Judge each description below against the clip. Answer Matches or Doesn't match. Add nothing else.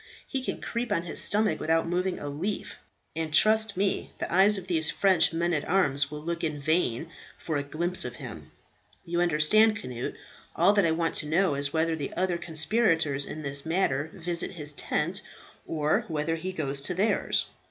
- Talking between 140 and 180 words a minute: Doesn't match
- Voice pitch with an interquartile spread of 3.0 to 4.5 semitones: Matches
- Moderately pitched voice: Matches